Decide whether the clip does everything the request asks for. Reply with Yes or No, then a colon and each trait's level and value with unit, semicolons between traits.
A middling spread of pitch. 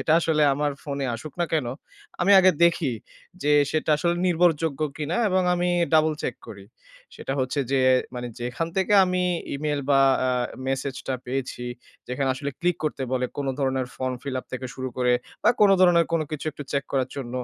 Yes: average, 4.1 semitones